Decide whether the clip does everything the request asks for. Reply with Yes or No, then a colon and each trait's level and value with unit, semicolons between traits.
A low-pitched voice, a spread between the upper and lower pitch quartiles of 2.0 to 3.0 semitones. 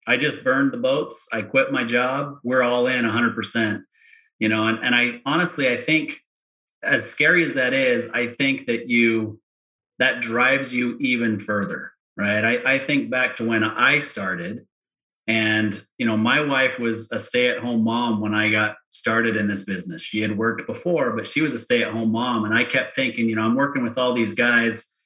Yes: low, 120 Hz; narrow, 2.5 semitones